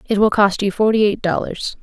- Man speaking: No, female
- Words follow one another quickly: Yes, fast, 230 wpm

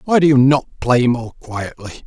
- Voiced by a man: Yes, male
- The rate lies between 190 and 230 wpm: Yes, fast, 205 wpm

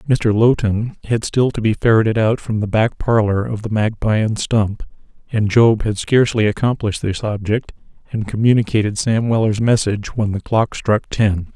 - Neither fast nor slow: Yes, average, 175 wpm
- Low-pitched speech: Yes, low, 110 Hz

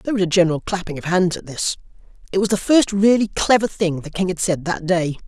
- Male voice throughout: Yes, male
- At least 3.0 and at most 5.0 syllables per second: No, 6.1 syllables/s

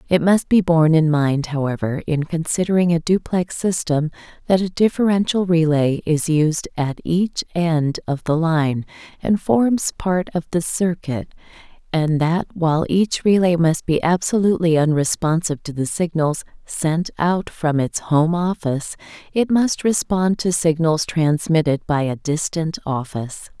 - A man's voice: No, female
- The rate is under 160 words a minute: Yes, average, 145 wpm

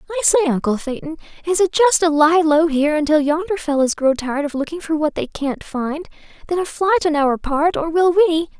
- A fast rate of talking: Yes, fast, 225 wpm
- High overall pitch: Yes, very high, 315 Hz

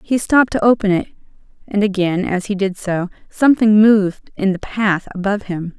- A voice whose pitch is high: Yes, high, 200 Hz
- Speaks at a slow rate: No, average, 185 wpm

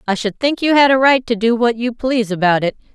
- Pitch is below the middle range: No, high, 235 Hz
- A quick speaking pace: Yes, fast, 285 wpm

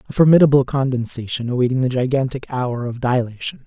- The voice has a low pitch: Yes, low, 130 Hz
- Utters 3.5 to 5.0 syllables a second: No, 6.1 syllables/s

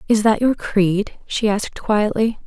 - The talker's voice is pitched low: No, high, 215 Hz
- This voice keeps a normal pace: Yes, average, 170 wpm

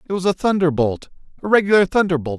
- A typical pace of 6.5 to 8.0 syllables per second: Yes, 6.6 syllables/s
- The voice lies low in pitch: No, medium, 175 Hz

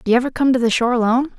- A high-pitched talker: Yes, high, 240 Hz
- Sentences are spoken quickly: Yes, fast, 350 wpm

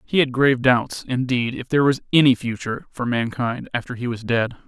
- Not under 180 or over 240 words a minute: Yes, fast, 205 wpm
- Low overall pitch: Yes, low, 125 Hz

